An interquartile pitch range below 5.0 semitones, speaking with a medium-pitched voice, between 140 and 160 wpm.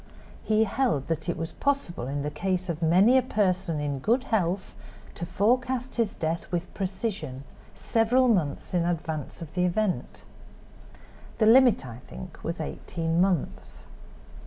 No: average, 5.3 semitones; medium, 180 Hz; average, 150 wpm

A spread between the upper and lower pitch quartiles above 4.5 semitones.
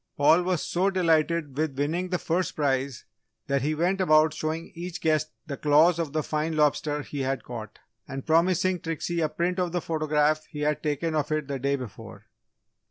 No: narrow, 2.6 semitones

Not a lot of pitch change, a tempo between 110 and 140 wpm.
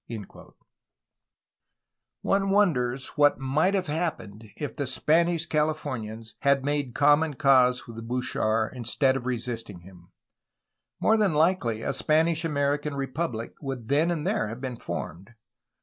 No: average, 4.7 semitones; slow, 135 wpm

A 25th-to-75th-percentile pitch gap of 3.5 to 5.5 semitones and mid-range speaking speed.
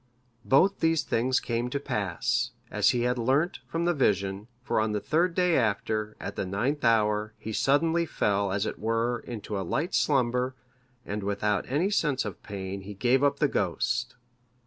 Yes: average, 5.2 semitones; average, 180 wpm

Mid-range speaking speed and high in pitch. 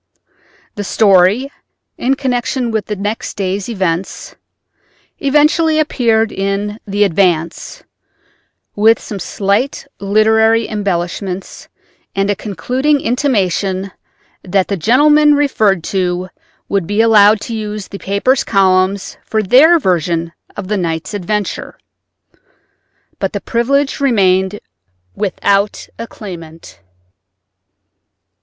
No: slow, 110 wpm; high, 205 Hz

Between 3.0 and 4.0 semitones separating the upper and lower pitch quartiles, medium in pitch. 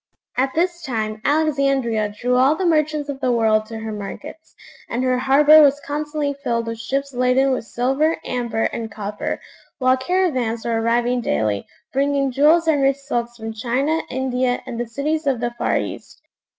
No: average, 3.6 semitones; very high, 260 Hz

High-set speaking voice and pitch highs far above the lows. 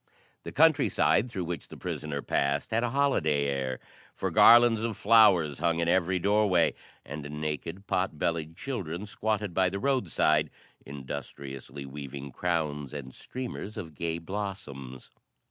No: very low, 85 Hz; wide, 6.4 semitones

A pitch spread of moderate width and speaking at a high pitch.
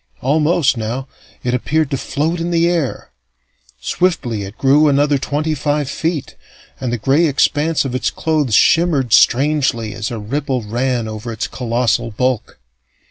No: average, 4.3 semitones; low, 135 Hz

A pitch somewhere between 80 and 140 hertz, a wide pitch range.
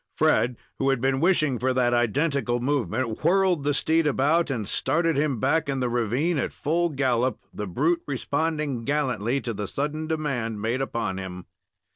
No: low, 135 Hz; average, 4.2 semitones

